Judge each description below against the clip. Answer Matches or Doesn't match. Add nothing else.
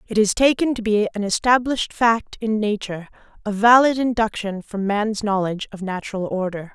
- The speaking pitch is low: Doesn't match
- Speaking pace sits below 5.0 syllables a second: Doesn't match